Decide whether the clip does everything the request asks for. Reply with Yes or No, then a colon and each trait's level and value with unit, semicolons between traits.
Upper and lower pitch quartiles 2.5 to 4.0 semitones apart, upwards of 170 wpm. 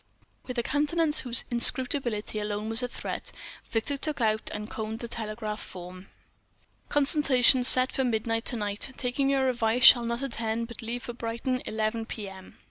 No: average, 2.9 semitones; average, 165 wpm